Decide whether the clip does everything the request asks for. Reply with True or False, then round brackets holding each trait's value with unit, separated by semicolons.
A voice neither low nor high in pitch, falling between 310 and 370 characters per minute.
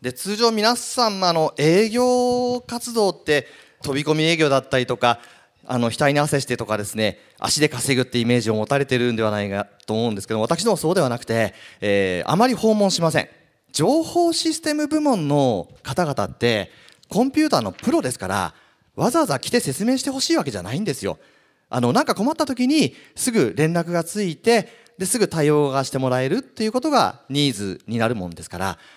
False (155 Hz; 390 characters per minute)